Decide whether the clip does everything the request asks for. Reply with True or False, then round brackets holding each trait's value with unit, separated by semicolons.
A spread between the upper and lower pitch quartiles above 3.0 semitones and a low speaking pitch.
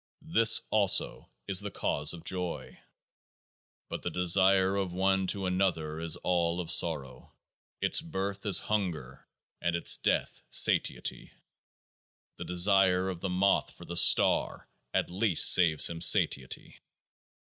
False (2.5 semitones; 90 Hz)